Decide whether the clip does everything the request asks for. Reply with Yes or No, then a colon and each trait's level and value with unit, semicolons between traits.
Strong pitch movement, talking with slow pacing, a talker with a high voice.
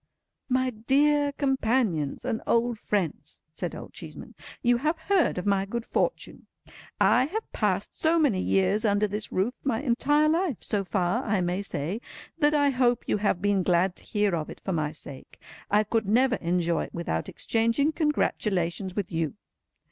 No: wide, 6.1 semitones; average, 165 wpm; high, 220 Hz